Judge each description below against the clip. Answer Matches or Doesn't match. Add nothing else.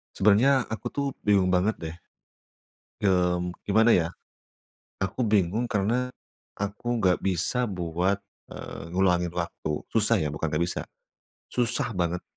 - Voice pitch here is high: Doesn't match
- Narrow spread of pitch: Doesn't match